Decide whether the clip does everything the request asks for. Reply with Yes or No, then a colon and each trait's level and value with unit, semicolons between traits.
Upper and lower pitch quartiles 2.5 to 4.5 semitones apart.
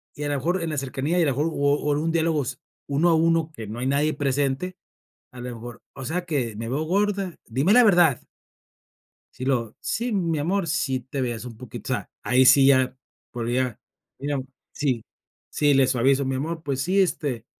Yes: average, 4.2 semitones